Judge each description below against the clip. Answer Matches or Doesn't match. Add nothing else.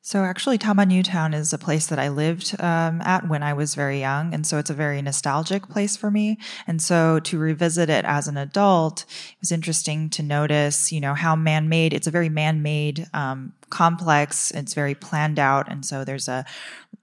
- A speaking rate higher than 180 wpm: Matches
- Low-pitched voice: Doesn't match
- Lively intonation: Doesn't match